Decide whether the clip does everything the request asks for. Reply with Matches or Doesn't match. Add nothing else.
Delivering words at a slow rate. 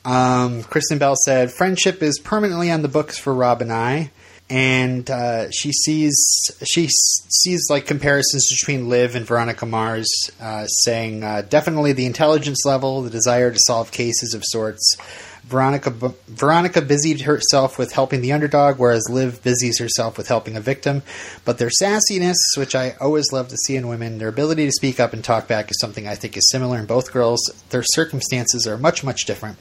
Doesn't match